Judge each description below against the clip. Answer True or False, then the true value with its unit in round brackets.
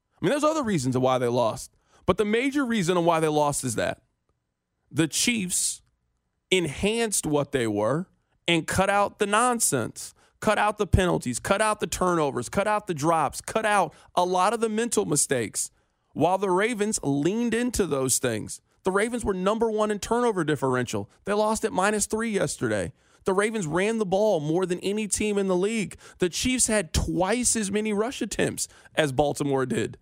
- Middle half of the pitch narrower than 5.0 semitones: False (5.5 semitones)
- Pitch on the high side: True (195 Hz)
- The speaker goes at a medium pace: True (185 wpm)